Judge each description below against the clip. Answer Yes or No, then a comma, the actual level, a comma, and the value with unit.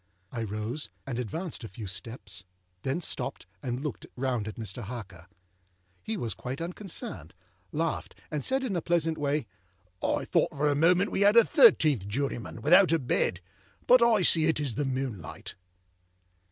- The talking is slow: No, average, 165 wpm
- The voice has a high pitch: No, low, 135 Hz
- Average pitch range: No, wide, 6.7 semitones